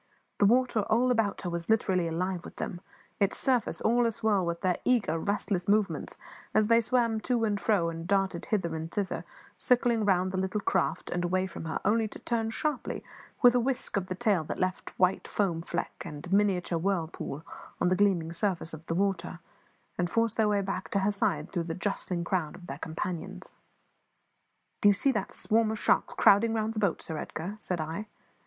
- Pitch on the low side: No, high, 195 Hz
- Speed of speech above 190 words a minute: Yes, fast, 205 wpm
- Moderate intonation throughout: Yes, average, 3.9 semitones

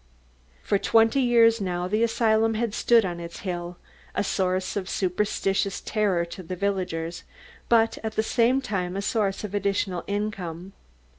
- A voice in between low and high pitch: No, high, 200 Hz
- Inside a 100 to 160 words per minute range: Yes, average, 155 wpm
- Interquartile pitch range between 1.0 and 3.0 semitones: No, average, 3.5 semitones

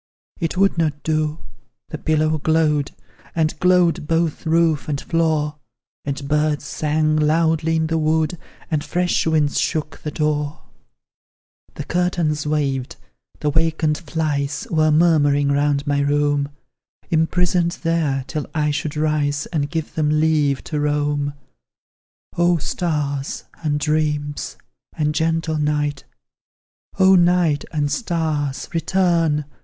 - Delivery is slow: Yes, slow, 125 wpm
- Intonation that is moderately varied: No, narrow, 1.8 semitones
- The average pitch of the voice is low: No, medium, 155 Hz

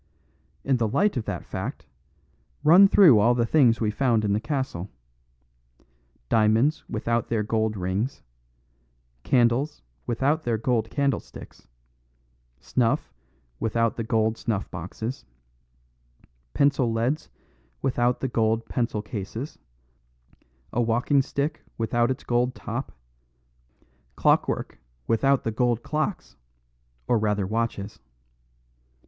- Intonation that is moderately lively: Yes, average, 3.2 semitones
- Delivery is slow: Yes, slow, 110 wpm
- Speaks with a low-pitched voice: Yes, low, 115 Hz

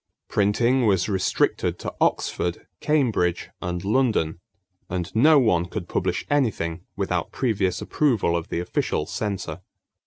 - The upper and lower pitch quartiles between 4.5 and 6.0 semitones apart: Yes, average, 5.3 semitones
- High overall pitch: No, low, 100 Hz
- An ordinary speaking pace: No, slow, 125 wpm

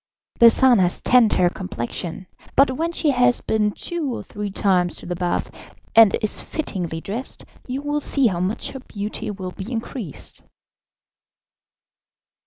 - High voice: Yes, high, 215 Hz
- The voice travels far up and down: Yes, wide, 5.8 semitones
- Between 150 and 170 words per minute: Yes, average, 155 wpm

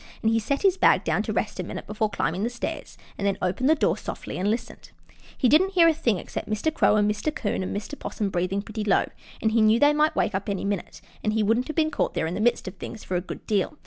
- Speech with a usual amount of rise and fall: No, wide, 5.8 semitones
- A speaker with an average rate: No, fast, 275 wpm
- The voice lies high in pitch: Yes, high, 215 Hz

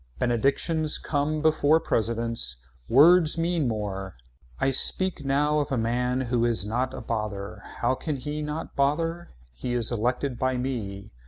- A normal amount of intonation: Yes, average, 4.5 semitones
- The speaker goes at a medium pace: Yes, average, 150 wpm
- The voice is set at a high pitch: No, low, 130 Hz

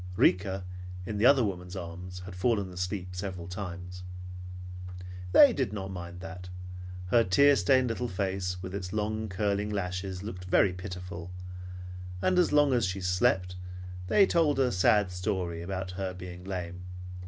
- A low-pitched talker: Yes, very low, 95 Hz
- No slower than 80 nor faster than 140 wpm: No, average, 155 wpm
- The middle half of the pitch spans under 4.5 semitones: Yes, narrow, 2.5 semitones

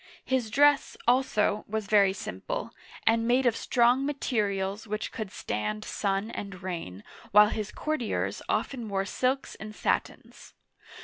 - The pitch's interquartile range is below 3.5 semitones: No, average, 4.0 semitones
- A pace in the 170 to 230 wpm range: No, average, 140 wpm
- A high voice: Yes, high, 215 Hz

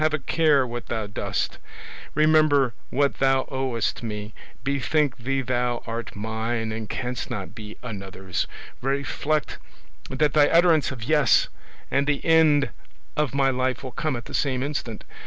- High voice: No, low, 130 Hz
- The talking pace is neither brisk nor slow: Yes, average, 155 wpm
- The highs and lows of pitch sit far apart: No, average, 4.0 semitones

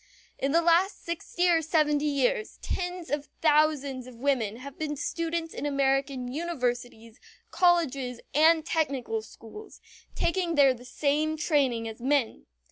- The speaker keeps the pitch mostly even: No, average, 4.4 semitones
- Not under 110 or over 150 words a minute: Yes, slow, 135 wpm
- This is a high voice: Yes, very high, 290 Hz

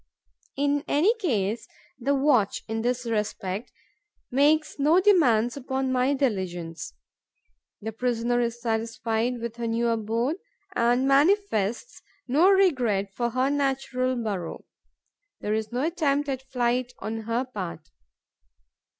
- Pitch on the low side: No, high, 245 Hz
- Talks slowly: Yes, slow, 125 wpm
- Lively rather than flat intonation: No, average, 3.8 semitones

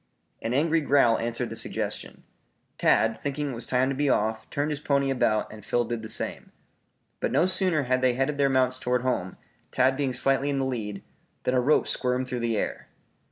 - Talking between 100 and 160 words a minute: No, fast, 205 wpm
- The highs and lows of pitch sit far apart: No, average, 2.7 semitones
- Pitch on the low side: Yes, low, 130 Hz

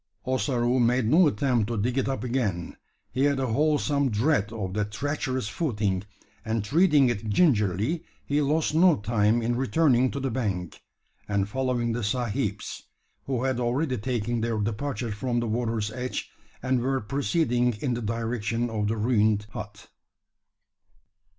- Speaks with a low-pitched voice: Yes, low, 120 Hz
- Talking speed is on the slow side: No, average, 155 wpm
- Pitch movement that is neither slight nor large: Yes, average, 3.8 semitones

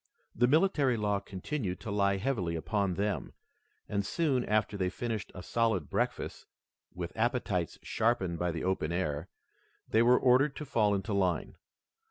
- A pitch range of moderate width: Yes, average, 4.8 semitones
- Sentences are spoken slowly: No, average, 155 wpm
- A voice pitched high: No, low, 105 Hz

